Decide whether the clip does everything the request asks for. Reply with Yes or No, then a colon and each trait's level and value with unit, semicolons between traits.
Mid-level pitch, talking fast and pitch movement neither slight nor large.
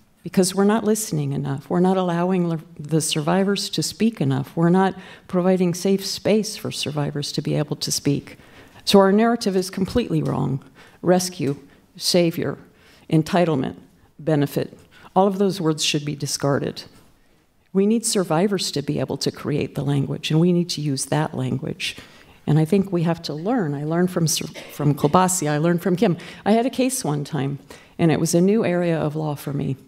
No: medium, 170 Hz; average, 185 wpm; average, 4.4 semitones